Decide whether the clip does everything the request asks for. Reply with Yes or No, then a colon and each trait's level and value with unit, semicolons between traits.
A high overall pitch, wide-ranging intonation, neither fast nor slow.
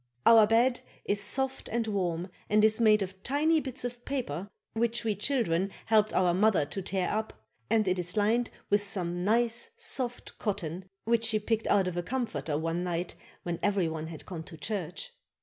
No: high, 205 Hz; average, 4.4 semitones; average, 185 wpm